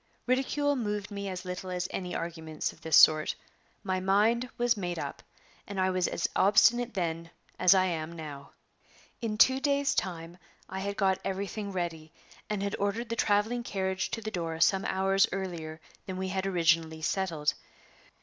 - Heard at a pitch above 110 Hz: Yes, high, 190 Hz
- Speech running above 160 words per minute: Yes, average, 170 wpm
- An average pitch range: Yes, average, 3.4 semitones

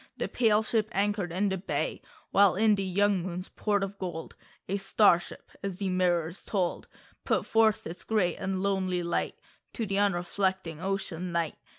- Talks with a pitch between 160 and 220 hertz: Yes, high, 190 Hz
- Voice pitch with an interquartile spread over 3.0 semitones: No, narrow, 2.4 semitones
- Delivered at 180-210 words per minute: Yes, average, 185 wpm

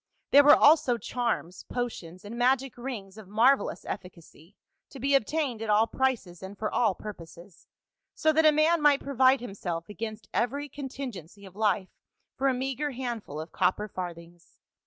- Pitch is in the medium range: No, high, 230 Hz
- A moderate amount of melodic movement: No, wide, 6.0 semitones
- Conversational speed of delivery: Yes, average, 170 wpm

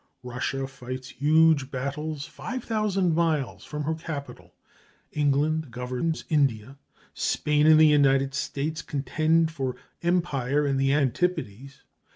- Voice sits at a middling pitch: Yes, medium, 145 Hz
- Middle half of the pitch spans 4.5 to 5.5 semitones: No, average, 2.8 semitones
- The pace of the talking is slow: Yes, slow, 120 wpm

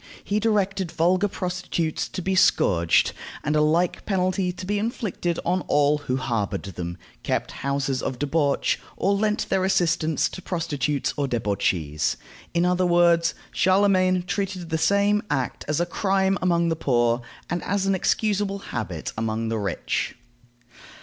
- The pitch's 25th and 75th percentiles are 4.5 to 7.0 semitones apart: Yes, wide, 5.5 semitones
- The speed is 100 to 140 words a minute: No, average, 150 wpm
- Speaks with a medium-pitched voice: Yes, medium, 170 Hz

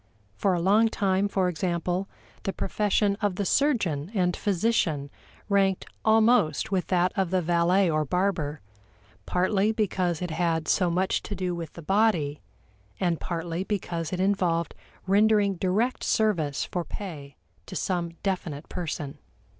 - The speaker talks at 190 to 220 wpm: No, average, 145 wpm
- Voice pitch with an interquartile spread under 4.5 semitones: Yes, average, 3.0 semitones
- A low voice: No, medium, 185 Hz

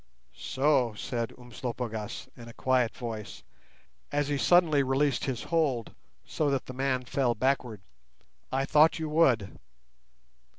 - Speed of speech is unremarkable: No, slow, 130 wpm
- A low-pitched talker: Yes, low, 130 Hz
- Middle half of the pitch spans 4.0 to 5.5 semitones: No, average, 3.5 semitones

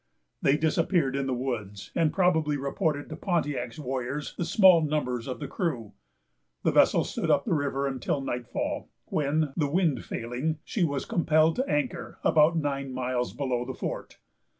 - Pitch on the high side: No, medium, 145 Hz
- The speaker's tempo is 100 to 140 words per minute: No, average, 165 wpm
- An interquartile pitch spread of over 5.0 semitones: No, average, 3.7 semitones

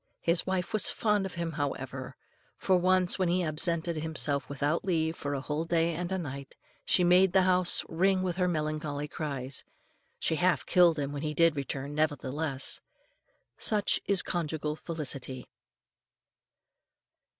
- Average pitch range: Yes, average, 3.6 semitones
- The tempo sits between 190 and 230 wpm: No, average, 150 wpm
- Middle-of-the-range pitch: Yes, medium, 160 Hz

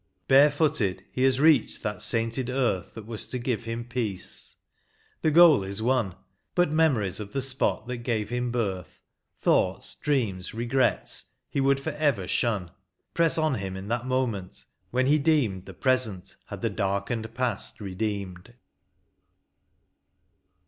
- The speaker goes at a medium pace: Yes, average, 145 wpm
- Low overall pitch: Yes, low, 120 Hz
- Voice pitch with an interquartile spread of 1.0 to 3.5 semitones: No, average, 4.8 semitones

